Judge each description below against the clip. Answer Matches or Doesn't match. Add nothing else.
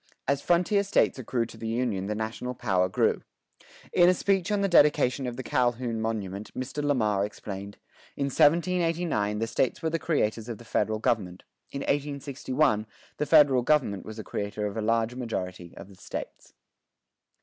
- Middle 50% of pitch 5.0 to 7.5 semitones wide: Matches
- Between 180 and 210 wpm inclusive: Doesn't match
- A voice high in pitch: Doesn't match